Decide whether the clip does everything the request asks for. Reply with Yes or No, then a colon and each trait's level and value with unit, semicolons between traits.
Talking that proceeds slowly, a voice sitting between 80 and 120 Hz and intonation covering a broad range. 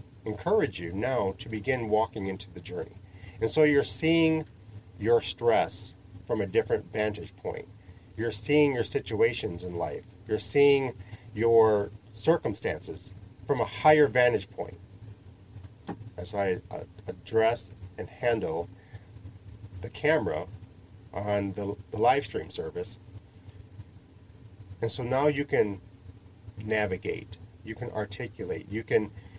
No: slow, 125 wpm; low, 105 Hz; narrow, 2.5 semitones